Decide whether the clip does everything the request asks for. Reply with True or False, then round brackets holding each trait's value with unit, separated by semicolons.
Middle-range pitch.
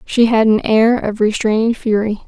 False (220 Hz)